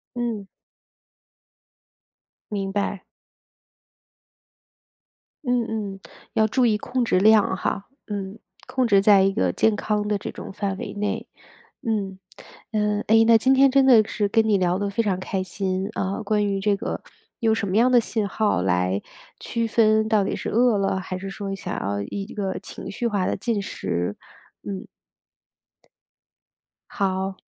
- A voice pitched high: Yes, high, 205 Hz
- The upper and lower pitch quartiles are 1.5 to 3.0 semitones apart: Yes, narrow, 2.4 semitones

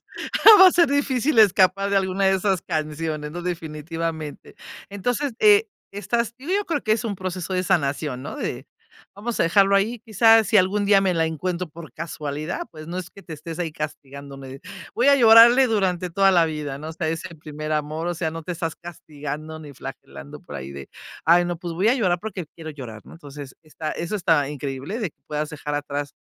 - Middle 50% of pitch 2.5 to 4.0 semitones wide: No, average, 4.7 semitones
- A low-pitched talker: No, medium, 170 Hz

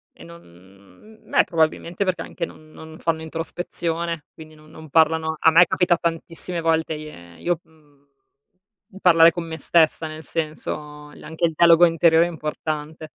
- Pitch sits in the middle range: Yes, medium, 160 Hz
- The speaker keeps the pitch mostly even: Yes, narrow, 1.3 semitones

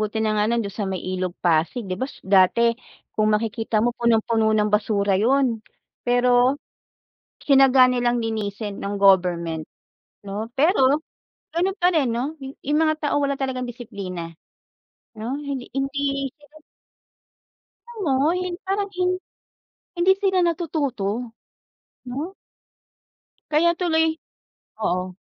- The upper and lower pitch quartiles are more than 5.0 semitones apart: Yes, wide, 5.4 semitones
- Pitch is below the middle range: No, high, 245 Hz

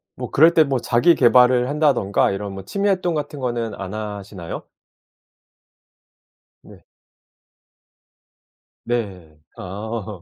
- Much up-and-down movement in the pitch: Yes, wide, 6.1 semitones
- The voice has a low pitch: Yes, low, 115 Hz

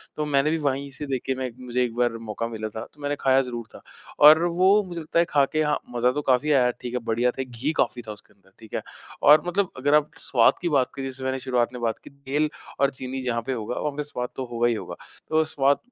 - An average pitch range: Yes, average, 3.4 semitones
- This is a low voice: Yes, low, 130 Hz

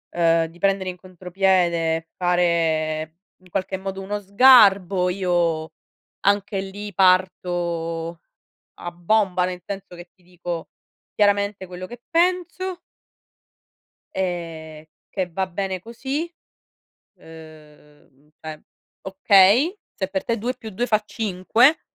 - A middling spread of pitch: Yes, average, 3.0 semitones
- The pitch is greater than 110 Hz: Yes, medium, 185 Hz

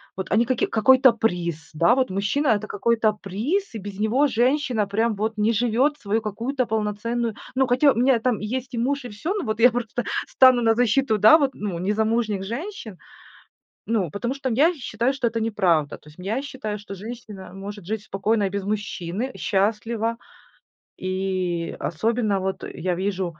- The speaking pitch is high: Yes, high, 220 Hz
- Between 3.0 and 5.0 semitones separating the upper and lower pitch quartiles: Yes, average, 3.6 semitones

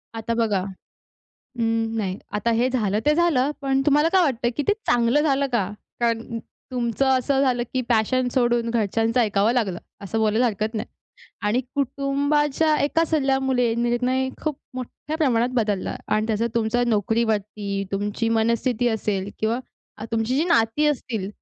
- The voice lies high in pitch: Yes, high, 235 Hz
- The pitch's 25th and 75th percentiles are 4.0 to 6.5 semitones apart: No, average, 3.3 semitones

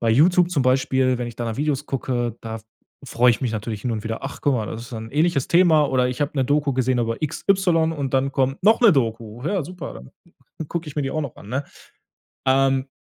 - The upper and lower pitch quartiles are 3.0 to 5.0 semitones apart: Yes, average, 4.1 semitones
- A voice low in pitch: Yes, low, 130 Hz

